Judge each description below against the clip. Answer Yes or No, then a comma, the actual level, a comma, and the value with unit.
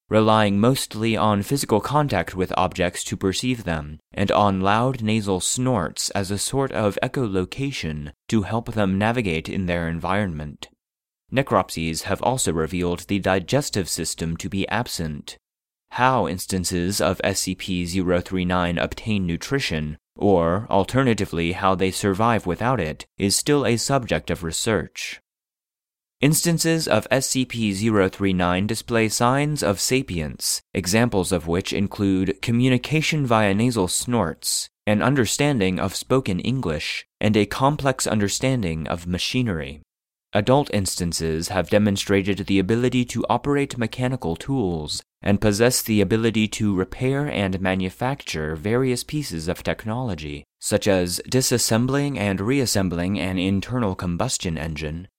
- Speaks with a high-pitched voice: No, low, 100 Hz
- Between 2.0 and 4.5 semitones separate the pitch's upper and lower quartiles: No, average, 5.3 semitones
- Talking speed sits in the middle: No, slow, 125 wpm